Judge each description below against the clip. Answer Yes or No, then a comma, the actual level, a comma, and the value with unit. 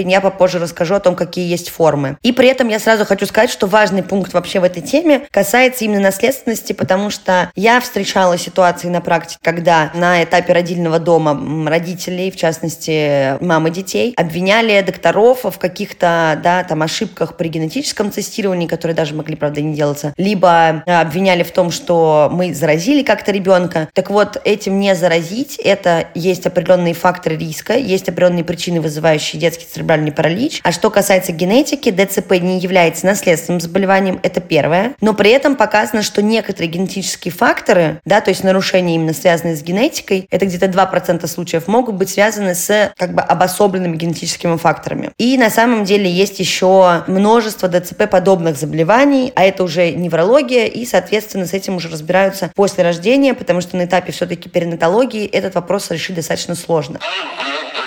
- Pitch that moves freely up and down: No, average, 3.2 semitones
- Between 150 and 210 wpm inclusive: Yes, fast, 160 wpm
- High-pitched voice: No, medium, 180 Hz